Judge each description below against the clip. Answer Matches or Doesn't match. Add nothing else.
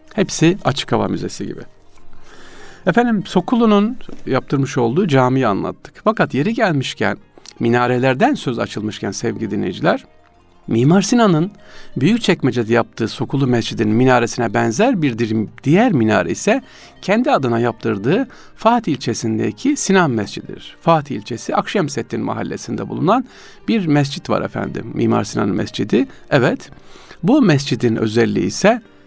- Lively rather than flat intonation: Matches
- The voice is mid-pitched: Doesn't match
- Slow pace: Doesn't match